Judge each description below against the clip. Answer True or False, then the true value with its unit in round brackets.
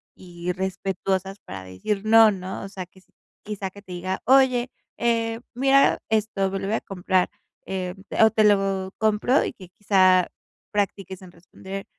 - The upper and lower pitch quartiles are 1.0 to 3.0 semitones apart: True (2.6 semitones)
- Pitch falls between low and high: False (195 Hz)